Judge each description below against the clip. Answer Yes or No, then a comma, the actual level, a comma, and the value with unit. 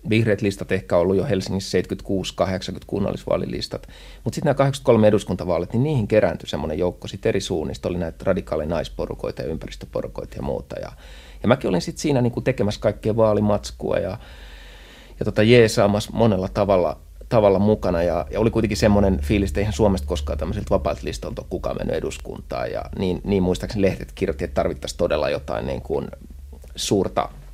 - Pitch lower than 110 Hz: Yes, low, 100 Hz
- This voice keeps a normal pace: No, fast, 170 wpm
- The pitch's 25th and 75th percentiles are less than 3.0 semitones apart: No, average, 3.5 semitones